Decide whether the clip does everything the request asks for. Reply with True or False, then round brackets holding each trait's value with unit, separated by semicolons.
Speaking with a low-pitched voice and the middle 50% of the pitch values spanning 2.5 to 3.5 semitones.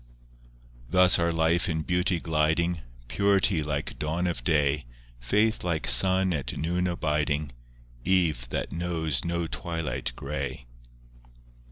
True (80 Hz; 2.9 semitones)